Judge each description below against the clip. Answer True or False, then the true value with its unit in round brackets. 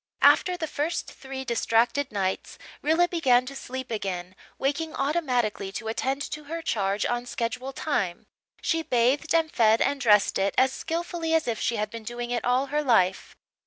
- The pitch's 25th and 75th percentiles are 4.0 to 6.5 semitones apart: True (5.1 semitones)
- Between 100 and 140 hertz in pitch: False (255 Hz)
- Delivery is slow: False (175 wpm)